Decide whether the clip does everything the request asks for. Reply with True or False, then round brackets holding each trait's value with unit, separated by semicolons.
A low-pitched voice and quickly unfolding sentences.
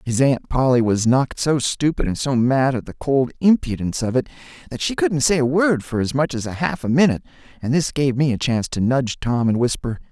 True (130 Hz; 245 wpm)